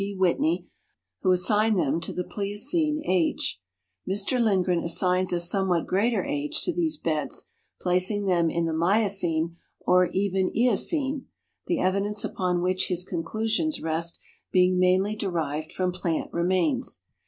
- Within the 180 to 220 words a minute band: No, average, 140 wpm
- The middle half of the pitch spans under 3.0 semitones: No, average, 3.6 semitones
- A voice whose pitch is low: No, medium, 185 Hz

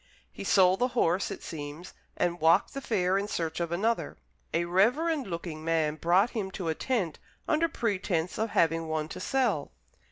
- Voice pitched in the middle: Yes, medium, 180 Hz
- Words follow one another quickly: No, average, 180 wpm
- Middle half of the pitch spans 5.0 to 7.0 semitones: Yes, average, 5.3 semitones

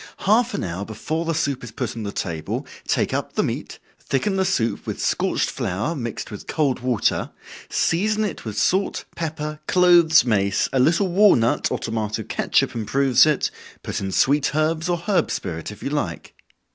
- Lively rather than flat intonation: Yes, wide, 7.5 semitones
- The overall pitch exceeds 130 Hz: Yes, medium, 140 Hz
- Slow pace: No, average, 180 wpm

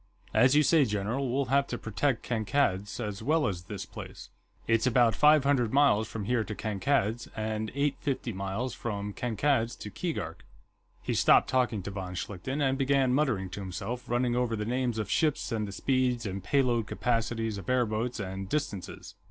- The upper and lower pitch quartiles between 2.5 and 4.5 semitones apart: Yes, average, 4.2 semitones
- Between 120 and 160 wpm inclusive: No, average, 185 wpm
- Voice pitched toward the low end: Yes, low, 115 Hz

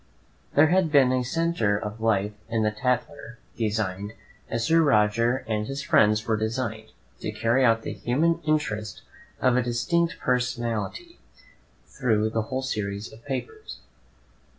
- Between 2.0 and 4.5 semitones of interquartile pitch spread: Yes, average, 4.1 semitones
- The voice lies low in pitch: Yes, low, 120 Hz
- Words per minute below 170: Yes, average, 140 wpm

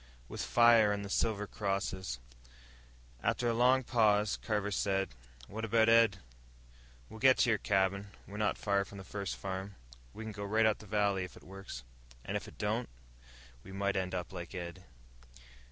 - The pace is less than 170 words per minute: No, average, 180 wpm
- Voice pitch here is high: No, low, 100 Hz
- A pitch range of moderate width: No, narrow, 2.3 semitones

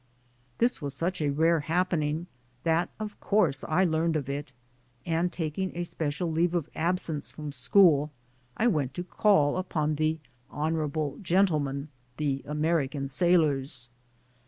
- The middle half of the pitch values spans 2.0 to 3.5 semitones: Yes, average, 3.2 semitones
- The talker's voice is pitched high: No, medium, 160 Hz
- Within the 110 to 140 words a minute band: Yes, slow, 135 wpm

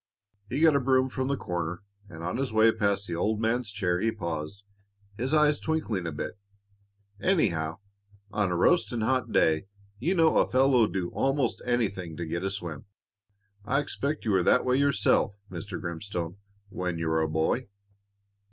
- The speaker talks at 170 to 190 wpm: Yes, average, 175 wpm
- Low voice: Yes, low, 105 Hz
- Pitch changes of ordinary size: No, wide, 7.0 semitones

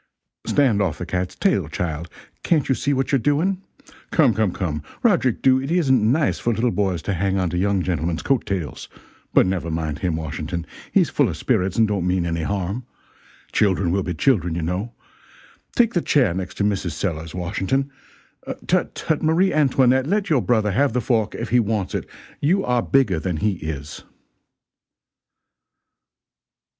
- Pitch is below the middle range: Yes, low, 100 Hz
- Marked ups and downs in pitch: Yes, wide, 7.0 semitones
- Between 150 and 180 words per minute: Yes, average, 175 wpm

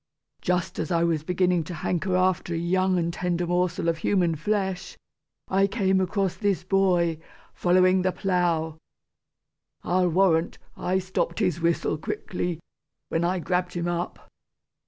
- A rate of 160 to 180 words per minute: No, average, 145 wpm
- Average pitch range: No, narrow, 1.7 semitones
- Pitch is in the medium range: Yes, medium, 180 Hz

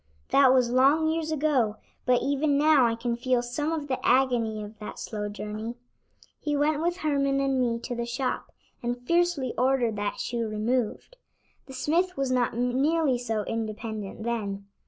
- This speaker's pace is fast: No, average, 170 wpm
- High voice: Yes, very high, 250 Hz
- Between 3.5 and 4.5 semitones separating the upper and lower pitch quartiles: Yes, average, 3.9 semitones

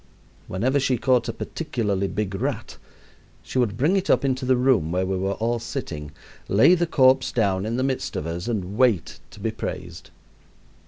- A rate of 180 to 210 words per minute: Yes, average, 190 wpm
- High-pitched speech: No, low, 115 Hz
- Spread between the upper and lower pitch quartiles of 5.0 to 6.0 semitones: Yes, average, 5.3 semitones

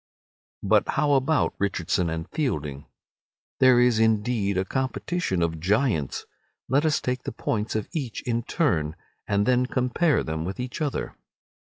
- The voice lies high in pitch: No, low, 115 Hz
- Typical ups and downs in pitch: No, wide, 6.1 semitones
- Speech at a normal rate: Yes, average, 150 wpm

